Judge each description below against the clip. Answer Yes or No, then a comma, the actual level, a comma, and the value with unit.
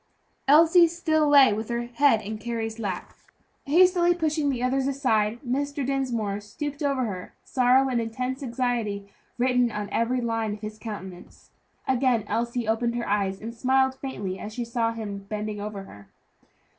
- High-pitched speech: Yes, high, 235 Hz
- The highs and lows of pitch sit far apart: No, average, 4.0 semitones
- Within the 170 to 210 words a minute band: No, average, 160 wpm